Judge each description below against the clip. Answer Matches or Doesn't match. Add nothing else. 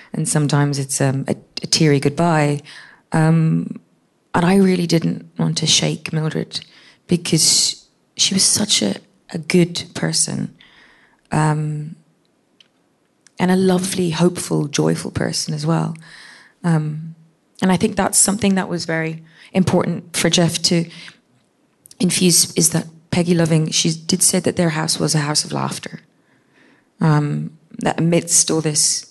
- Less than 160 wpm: Matches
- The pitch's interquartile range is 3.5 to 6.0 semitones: Doesn't match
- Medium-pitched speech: Matches